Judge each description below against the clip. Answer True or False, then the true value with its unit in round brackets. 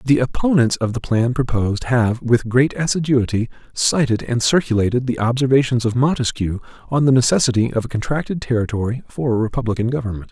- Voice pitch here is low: True (125 Hz)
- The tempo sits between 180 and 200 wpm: False (165 wpm)